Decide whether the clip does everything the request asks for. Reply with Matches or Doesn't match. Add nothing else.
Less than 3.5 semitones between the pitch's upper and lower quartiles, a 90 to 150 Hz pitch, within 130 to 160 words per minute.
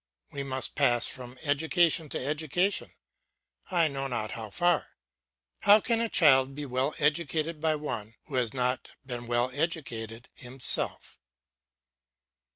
Doesn't match